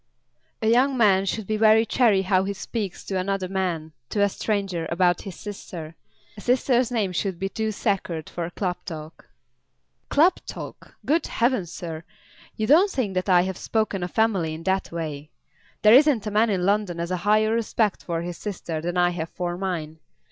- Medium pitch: No, high, 195 Hz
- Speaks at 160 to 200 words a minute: Yes, average, 190 wpm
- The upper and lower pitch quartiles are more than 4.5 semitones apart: No, average, 3.8 semitones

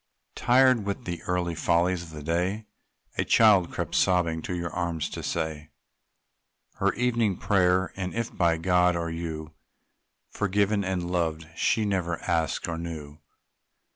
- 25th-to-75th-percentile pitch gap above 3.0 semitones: No, average, 2.7 semitones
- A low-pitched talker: Yes, very low, 90 Hz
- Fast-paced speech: No, average, 145 wpm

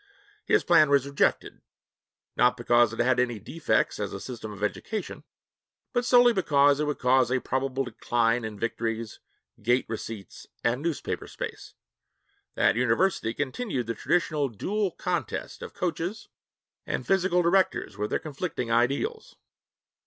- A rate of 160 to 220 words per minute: No, average, 140 wpm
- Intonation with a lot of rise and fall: Yes, wide, 6.7 semitones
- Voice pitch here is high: No, low, 130 Hz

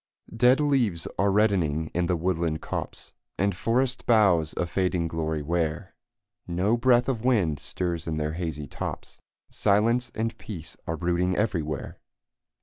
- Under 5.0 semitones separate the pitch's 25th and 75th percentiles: No, wide, 5.4 semitones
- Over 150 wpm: No, average, 145 wpm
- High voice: No, very low, 90 Hz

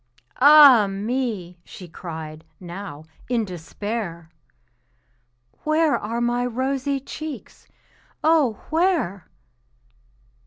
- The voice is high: Yes, high, 230 Hz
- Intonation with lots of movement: Yes, wide, 7.4 semitones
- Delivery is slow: Yes, slow, 80 wpm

